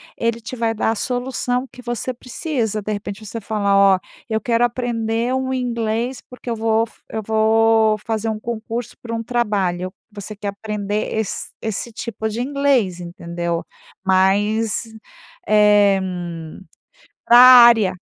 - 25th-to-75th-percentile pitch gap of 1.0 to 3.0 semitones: Yes, narrow, 2.5 semitones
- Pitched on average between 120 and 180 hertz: No, high, 220 Hz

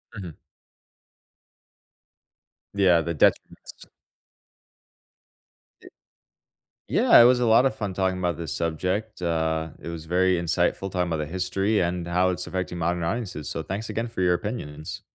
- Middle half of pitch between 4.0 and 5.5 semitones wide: No, average, 2.8 semitones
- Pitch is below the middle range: Yes, very low, 90 Hz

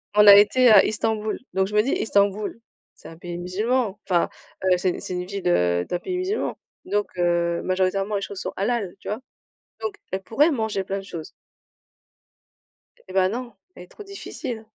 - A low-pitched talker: No, high, 200 Hz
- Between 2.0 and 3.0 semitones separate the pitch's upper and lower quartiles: No, average, 3.4 semitones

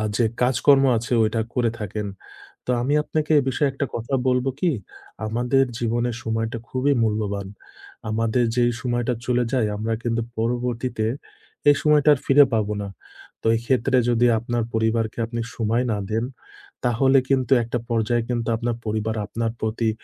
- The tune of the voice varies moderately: No, narrow, 2.1 semitones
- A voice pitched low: Yes, low, 120 Hz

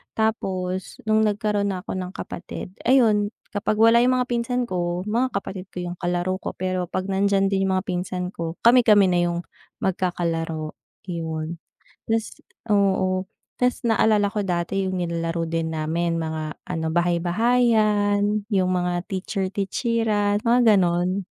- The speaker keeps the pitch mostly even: No, average, 3.3 semitones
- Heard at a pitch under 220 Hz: Yes, high, 190 Hz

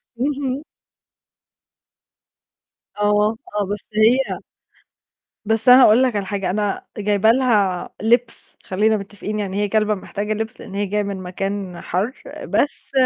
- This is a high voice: Yes, high, 210 Hz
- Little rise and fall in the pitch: Yes, narrow, 2.0 semitones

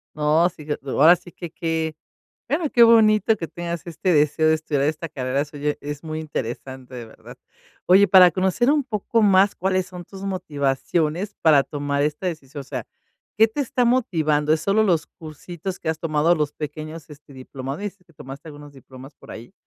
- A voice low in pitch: No, medium, 160 Hz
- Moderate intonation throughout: Yes, average, 4.2 semitones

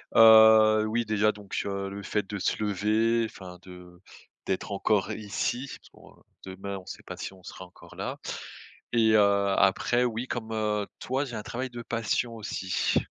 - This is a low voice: Yes, low, 105 Hz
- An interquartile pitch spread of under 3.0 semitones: Yes, narrow, 2.6 semitones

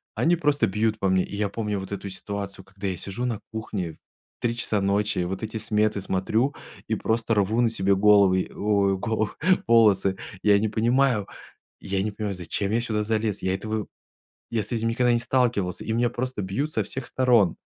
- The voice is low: Yes, low, 105 Hz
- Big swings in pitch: No, average, 2.8 semitones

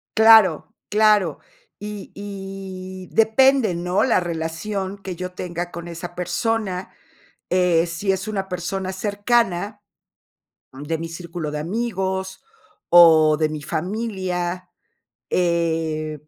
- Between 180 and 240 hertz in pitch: Yes, medium, 185 Hz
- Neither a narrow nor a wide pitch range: Yes, average, 3.0 semitones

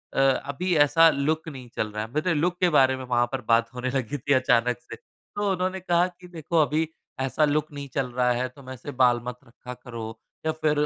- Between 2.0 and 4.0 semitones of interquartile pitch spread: No, average, 4.4 semitones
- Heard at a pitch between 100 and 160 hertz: Yes, medium, 140 Hz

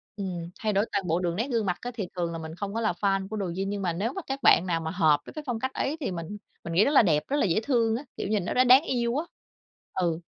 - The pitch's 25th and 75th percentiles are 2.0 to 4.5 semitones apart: No, average, 5.3 semitones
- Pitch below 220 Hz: Yes, high, 200 Hz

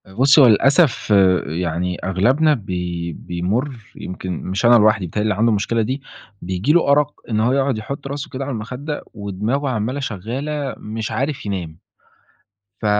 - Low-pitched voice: Yes, low, 115 Hz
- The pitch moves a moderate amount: No, wide, 6.3 semitones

